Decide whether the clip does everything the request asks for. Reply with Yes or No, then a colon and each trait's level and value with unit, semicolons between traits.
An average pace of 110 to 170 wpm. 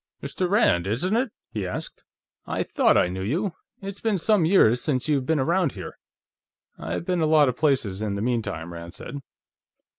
No: average, 185 wpm